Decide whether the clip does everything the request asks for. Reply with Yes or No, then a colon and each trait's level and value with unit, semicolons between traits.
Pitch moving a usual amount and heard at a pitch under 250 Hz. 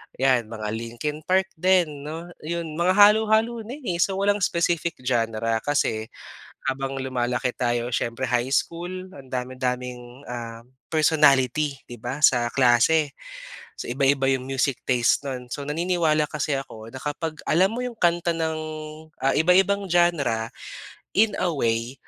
No: wide, 5.7 semitones; medium, 140 Hz